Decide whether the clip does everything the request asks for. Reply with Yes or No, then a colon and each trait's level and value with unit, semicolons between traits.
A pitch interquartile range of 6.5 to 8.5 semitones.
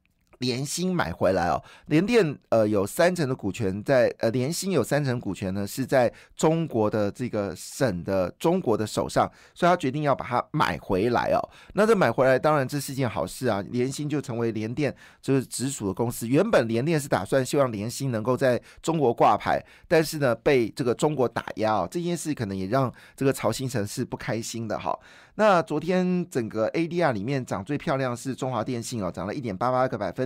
No: average, 5.2 semitones